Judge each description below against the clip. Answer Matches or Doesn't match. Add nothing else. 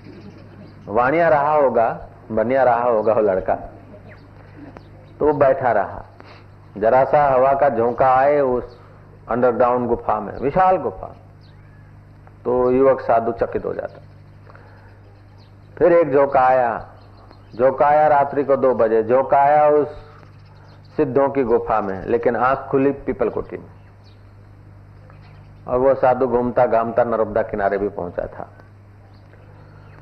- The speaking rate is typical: Matches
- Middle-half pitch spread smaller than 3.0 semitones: Doesn't match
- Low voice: Matches